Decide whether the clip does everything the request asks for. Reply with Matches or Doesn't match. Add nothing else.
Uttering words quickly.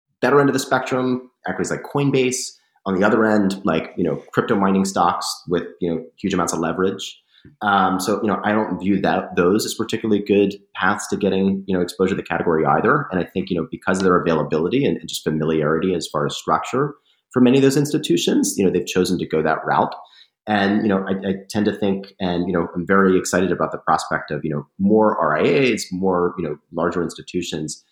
Matches